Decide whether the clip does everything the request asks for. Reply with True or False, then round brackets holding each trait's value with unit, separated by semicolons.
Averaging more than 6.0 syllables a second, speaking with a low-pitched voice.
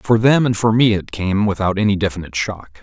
False (5.7 syllables/s; 105 Hz)